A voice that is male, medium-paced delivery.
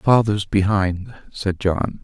No: male; slow, 120 wpm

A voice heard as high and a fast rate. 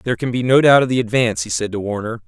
No: low, 115 Hz; fast, 315 wpm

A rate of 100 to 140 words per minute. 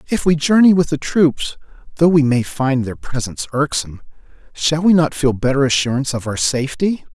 No: average, 185 wpm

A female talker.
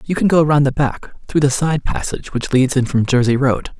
No: male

